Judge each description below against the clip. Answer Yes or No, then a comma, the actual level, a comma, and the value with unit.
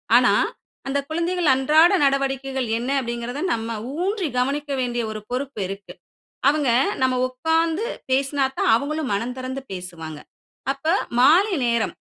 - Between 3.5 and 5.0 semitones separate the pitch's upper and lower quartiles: Yes, average, 4.0 semitones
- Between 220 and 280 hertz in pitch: Yes, very high, 270 Hz